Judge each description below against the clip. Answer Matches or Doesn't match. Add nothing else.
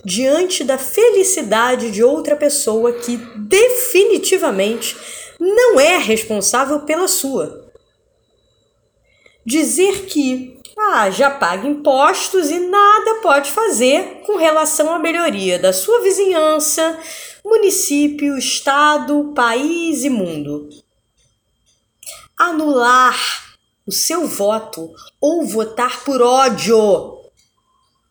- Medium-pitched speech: Doesn't match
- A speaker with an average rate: Doesn't match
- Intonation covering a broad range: Matches